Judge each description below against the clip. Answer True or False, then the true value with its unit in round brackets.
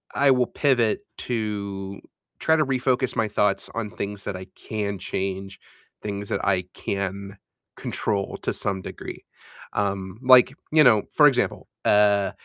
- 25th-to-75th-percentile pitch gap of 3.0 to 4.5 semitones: True (4.1 semitones)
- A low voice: True (105 Hz)